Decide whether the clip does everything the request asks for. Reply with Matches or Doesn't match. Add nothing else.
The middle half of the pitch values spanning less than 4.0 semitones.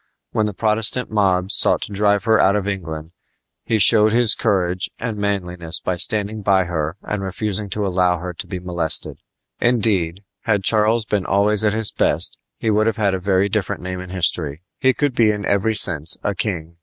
Matches